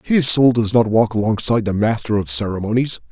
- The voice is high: No, low, 110 Hz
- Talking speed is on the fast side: No, average, 195 wpm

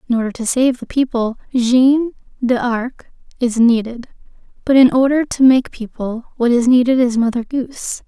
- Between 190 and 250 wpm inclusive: No, average, 165 wpm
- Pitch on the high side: Yes, high, 245 Hz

